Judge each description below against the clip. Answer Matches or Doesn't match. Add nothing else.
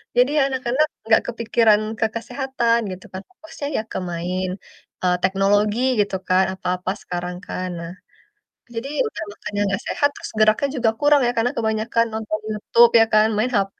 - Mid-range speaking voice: Doesn't match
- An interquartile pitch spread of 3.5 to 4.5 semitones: Matches